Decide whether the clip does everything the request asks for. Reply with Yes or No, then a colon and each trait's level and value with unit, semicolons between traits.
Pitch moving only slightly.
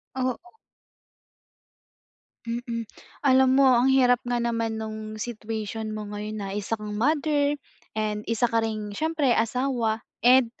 No: average, 3.1 semitones